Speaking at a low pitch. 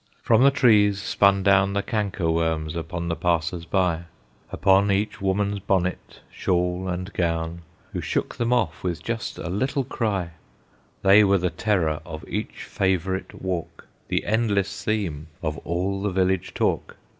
Yes: very low, 95 Hz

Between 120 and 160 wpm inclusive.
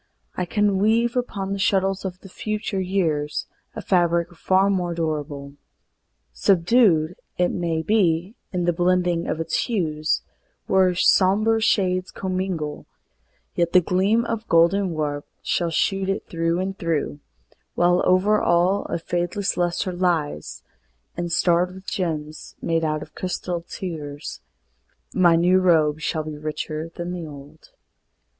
Yes: average, 140 wpm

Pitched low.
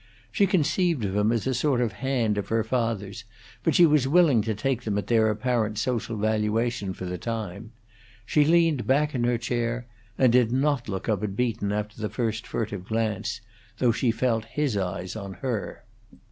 Yes: low, 115 Hz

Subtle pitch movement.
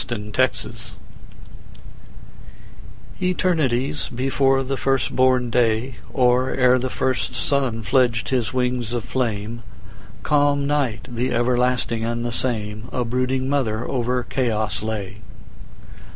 Yes: narrow, 2.1 semitones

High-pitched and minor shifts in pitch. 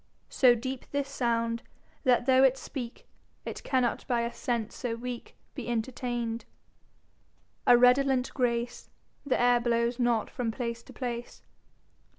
Yes: high, 245 Hz; narrow, 1.5 semitones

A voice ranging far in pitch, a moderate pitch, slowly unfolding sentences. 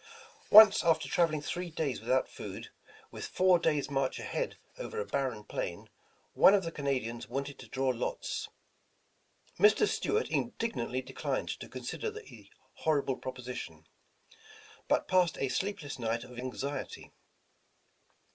Yes: wide, 6.3 semitones; medium, 145 Hz; slow, 130 wpm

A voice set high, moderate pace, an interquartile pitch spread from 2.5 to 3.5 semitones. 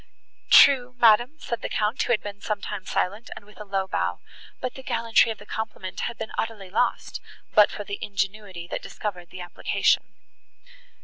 Yes: high, 210 Hz; average, 185 wpm; average, 2.9 semitones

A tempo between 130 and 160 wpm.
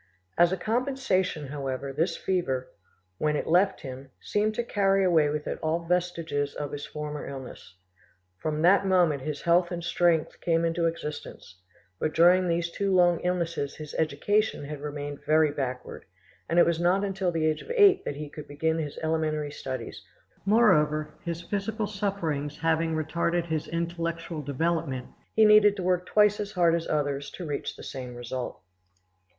No: average, 170 wpm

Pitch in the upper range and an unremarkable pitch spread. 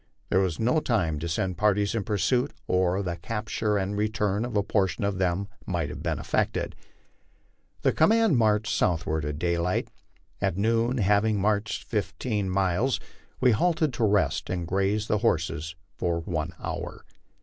No: low, 100 Hz; average, 3.7 semitones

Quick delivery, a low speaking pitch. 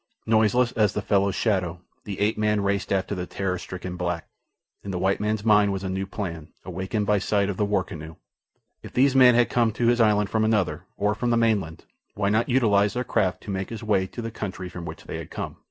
Yes: fast, 235 wpm; low, 100 Hz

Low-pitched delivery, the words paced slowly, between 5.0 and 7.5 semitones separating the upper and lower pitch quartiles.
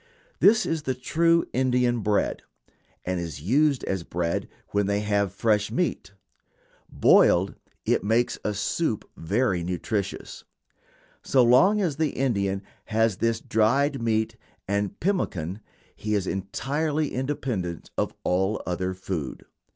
Yes: low, 110 Hz; slow, 130 wpm; wide, 5.6 semitones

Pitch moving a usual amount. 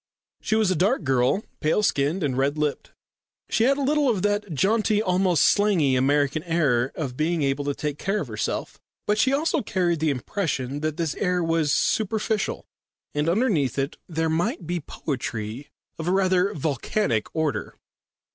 No: wide, 6.2 semitones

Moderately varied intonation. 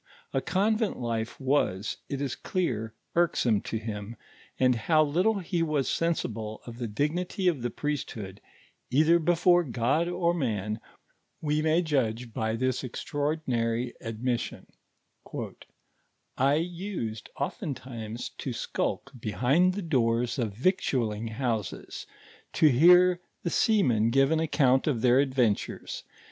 No: wide, 6.4 semitones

